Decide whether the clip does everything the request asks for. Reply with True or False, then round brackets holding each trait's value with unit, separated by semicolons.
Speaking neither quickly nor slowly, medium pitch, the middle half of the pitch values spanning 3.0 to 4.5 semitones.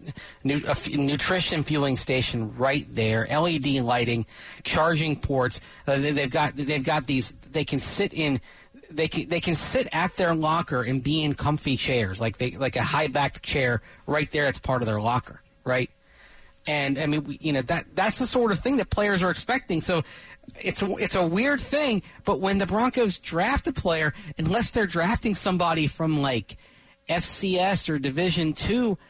False (175 wpm; 155 Hz; 5.1 semitones)